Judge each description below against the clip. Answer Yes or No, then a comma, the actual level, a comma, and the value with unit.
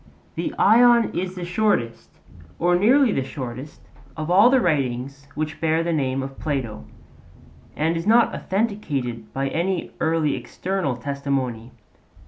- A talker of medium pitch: Yes, medium, 155 Hz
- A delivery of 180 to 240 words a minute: No, slow, 135 wpm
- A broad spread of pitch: Yes, wide, 5.9 semitones